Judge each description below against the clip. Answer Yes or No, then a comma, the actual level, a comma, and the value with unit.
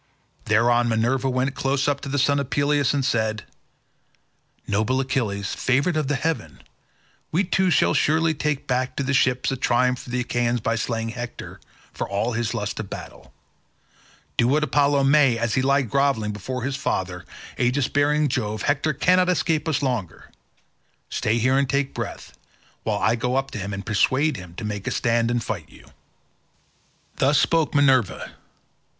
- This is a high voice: No, low, 130 Hz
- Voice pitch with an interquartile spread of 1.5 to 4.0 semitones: Yes, average, 3.6 semitones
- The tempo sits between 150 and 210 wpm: Yes, average, 170 wpm